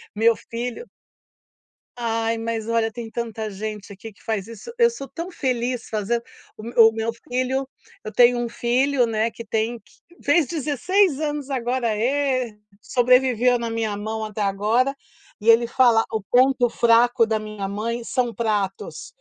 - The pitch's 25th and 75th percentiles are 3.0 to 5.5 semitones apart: No, narrow, 2.5 semitones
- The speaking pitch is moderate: No, high, 235 Hz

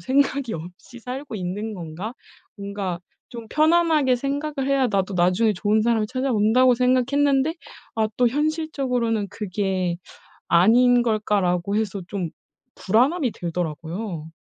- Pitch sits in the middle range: No, high, 225 Hz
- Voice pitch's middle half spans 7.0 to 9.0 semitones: No, wide, 5.5 semitones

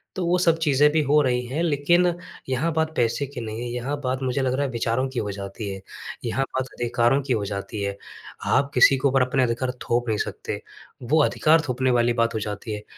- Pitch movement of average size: Yes, average, 3.5 semitones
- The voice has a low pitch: Yes, low, 130 Hz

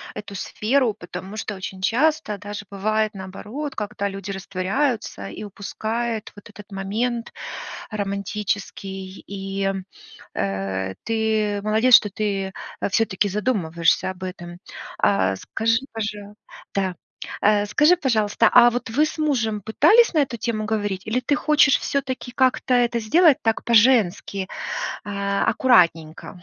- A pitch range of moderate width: Yes, average, 3.4 semitones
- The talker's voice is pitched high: Yes, high, 210 Hz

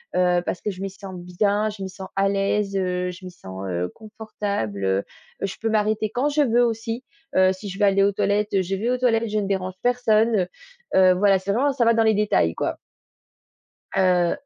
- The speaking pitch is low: No, high, 200 Hz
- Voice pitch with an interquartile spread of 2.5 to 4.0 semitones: Yes, average, 2.8 semitones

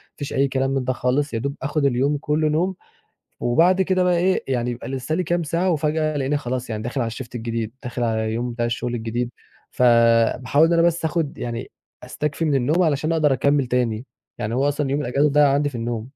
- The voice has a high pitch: No, low, 135 Hz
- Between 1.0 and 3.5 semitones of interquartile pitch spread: No, average, 4.1 semitones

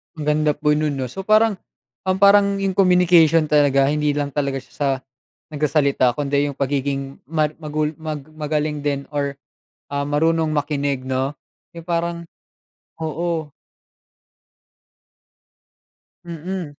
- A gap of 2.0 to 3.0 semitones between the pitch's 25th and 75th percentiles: Yes, narrow, 2.6 semitones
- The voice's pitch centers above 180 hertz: No, medium, 150 Hz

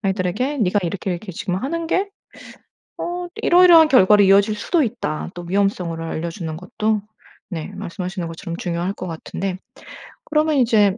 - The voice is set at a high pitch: Yes, high, 195 Hz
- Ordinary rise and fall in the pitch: No, wide, 6.3 semitones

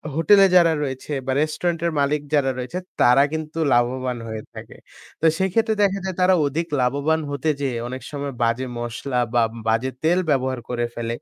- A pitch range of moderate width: Yes, average, 4.6 semitones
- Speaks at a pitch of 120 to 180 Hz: Yes, medium, 140 Hz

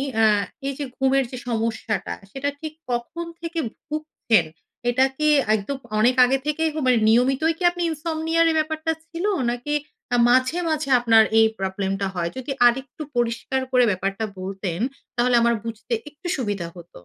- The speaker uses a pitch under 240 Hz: No, very high, 250 Hz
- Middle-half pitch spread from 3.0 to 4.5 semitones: No, wide, 5.6 semitones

